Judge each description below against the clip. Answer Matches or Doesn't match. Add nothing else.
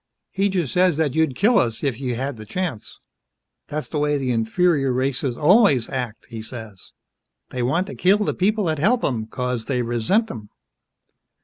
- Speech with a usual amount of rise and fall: Doesn't match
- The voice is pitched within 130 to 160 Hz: Matches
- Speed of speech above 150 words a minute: Matches